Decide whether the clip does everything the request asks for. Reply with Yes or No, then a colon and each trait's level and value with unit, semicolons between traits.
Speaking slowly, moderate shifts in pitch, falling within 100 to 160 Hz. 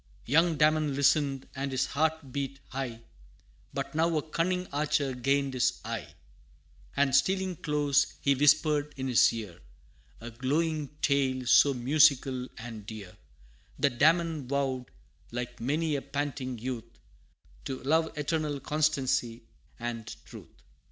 Yes: slow, 130 wpm; average, 3.2 semitones; medium, 140 Hz